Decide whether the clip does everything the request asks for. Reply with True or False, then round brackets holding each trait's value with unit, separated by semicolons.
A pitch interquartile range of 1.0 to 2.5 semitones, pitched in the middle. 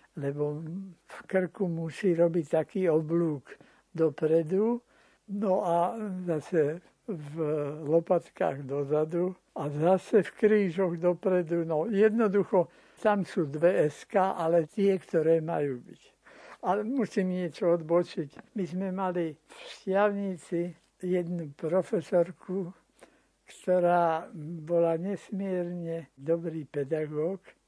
False (2.9 semitones; 175 Hz)